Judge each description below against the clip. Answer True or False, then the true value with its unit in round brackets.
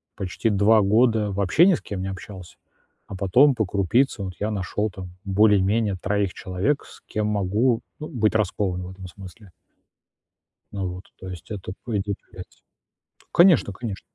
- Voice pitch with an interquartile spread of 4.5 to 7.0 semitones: False (2.8 semitones)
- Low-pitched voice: True (100 Hz)